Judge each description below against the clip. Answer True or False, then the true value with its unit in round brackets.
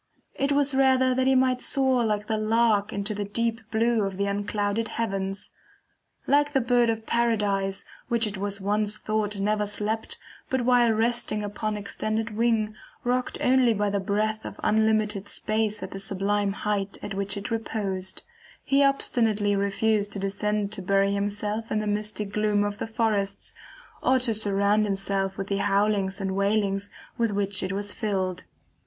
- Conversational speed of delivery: True (170 wpm)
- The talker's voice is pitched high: True (210 Hz)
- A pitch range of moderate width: False (2.2 semitones)